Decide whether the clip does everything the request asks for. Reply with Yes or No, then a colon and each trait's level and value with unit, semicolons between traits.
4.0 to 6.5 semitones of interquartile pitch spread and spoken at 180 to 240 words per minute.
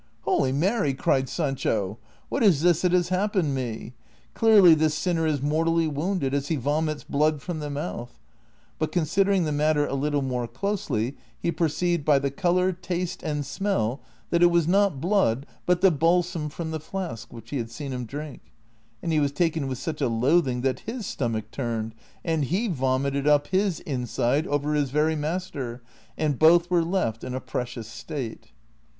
Yes: average, 4.6 semitones; average, 190 wpm